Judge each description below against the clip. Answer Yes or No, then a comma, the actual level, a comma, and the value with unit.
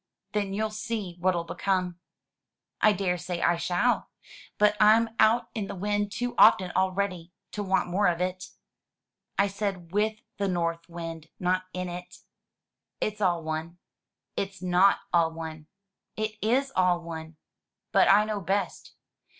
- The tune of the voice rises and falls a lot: No, average, 3.1 semitones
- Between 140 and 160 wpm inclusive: Yes, average, 150 wpm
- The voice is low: No, medium, 185 Hz